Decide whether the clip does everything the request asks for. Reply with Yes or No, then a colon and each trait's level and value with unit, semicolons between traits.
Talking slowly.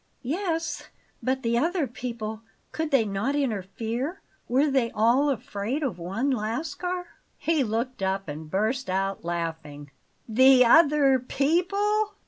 Yes: slow, 125 wpm